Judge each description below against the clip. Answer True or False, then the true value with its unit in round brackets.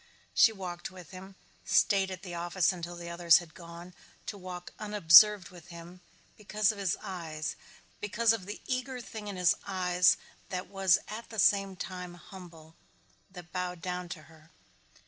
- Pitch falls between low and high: True (180 Hz)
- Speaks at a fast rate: False (165 wpm)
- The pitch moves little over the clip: True (2.2 semitones)